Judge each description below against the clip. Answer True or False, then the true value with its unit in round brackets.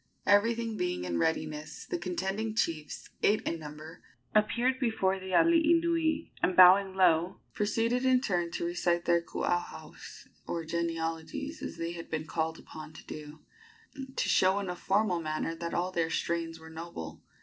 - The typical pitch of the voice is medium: True (175 Hz)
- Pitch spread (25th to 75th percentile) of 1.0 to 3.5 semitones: False (4.5 semitones)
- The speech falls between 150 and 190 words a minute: True (160 wpm)